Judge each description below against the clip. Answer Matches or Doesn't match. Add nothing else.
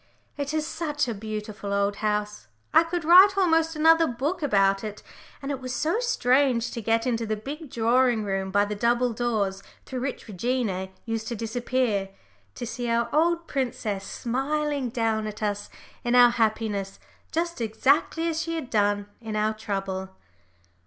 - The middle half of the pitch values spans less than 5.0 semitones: Doesn't match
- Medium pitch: Doesn't match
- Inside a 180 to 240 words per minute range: Doesn't match